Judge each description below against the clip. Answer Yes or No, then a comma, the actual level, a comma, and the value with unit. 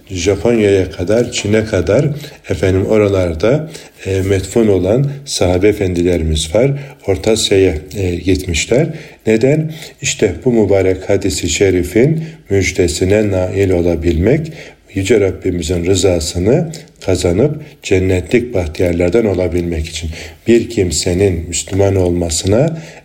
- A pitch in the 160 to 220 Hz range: No, very low, 95 Hz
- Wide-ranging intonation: No, average, 4.7 semitones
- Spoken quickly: No, slow, 95 wpm